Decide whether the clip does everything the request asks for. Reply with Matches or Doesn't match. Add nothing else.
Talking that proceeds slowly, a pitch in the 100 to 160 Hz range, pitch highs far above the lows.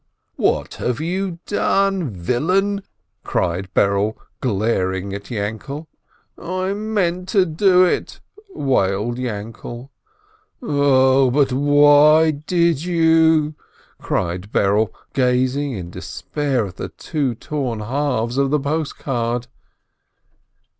Matches